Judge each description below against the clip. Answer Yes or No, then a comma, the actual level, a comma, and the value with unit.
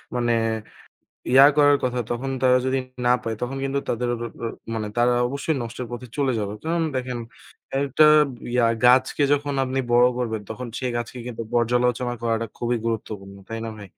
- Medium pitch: No, low, 125 Hz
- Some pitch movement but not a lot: No, narrow, 2.1 semitones